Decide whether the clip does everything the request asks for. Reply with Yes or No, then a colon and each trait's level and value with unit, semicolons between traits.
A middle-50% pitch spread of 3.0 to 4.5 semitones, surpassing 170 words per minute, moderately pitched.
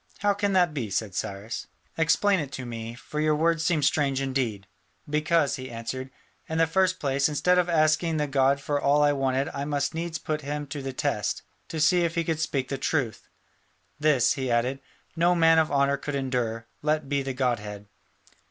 Yes: average, 3.6 semitones; average, 200 wpm; medium, 145 Hz